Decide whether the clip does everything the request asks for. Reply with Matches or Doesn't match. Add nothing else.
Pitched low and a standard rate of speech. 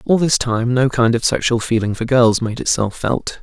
Doesn't match